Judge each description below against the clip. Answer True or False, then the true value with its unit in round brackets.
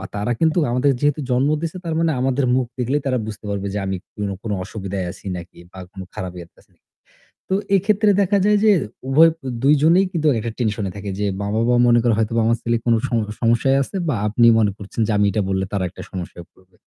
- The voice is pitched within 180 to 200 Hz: False (115 Hz)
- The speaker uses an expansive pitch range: True (6.3 semitones)